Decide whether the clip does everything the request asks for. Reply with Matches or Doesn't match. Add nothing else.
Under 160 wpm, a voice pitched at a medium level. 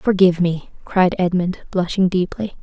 Matches